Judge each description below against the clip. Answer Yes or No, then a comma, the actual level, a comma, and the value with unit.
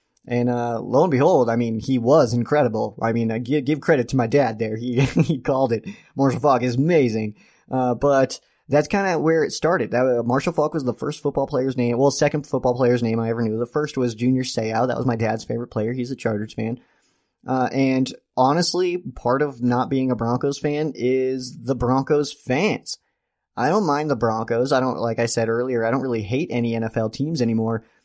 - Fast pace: Yes, fast, 220 wpm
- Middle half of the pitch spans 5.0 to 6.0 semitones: No, average, 3.2 semitones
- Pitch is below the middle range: Yes, low, 125 Hz